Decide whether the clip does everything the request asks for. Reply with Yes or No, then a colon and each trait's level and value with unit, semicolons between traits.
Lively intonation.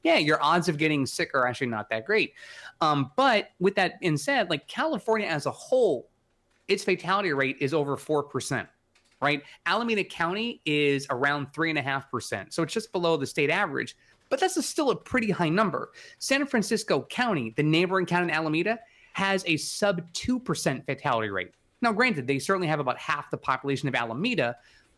Yes: wide, 7.0 semitones